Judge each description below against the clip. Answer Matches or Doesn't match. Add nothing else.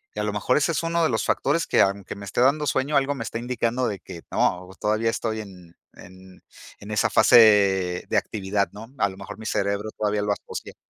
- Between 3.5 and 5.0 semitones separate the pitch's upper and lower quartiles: Matches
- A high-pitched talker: Doesn't match